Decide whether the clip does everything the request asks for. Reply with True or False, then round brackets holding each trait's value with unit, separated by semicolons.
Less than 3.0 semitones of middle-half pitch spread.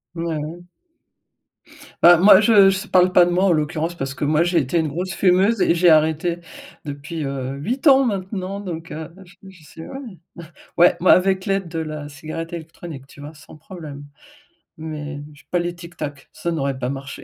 False (3.3 semitones)